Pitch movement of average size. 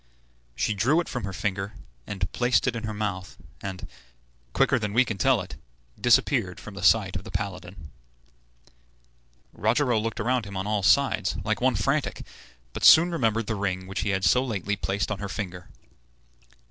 Yes: average, 3.4 semitones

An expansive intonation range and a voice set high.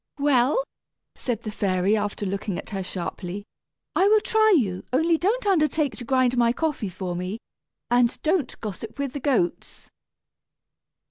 Yes: wide, 7.3 semitones; high, 245 Hz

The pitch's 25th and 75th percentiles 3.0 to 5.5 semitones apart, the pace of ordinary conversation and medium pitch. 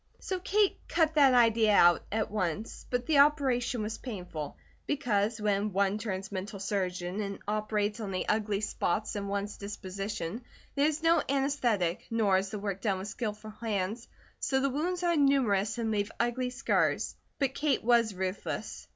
No: average, 4.2 semitones; average, 170 wpm; high, 215 Hz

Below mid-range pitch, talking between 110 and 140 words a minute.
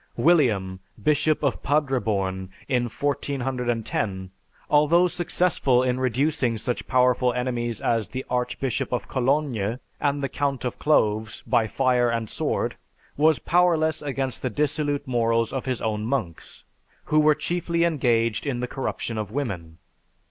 Yes: low, 125 Hz; slow, 135 wpm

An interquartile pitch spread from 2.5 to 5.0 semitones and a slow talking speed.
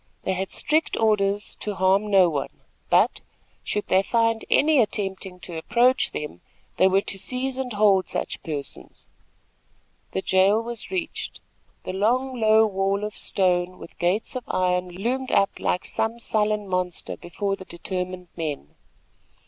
No: average, 3.5 semitones; average, 155 wpm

